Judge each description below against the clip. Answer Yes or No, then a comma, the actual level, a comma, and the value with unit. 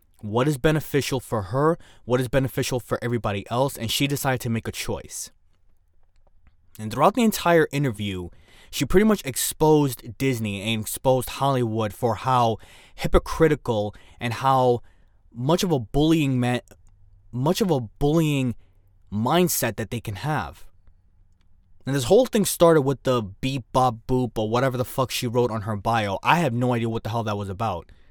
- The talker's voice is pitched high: No, low, 120 Hz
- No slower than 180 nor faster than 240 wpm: No, average, 170 wpm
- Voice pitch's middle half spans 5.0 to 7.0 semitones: Yes, average, 5.3 semitones